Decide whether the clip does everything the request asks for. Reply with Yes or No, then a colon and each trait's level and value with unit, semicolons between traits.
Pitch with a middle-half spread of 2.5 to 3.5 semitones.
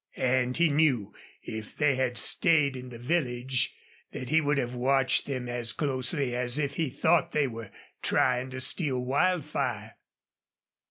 Yes: average, 2.9 semitones